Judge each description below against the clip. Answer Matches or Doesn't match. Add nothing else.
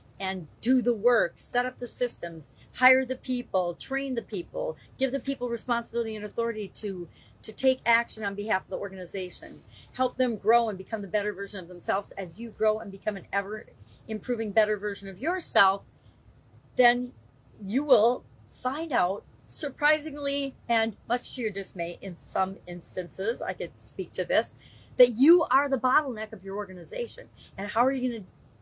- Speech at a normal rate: Matches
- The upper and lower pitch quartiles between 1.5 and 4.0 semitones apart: Doesn't match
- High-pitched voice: Matches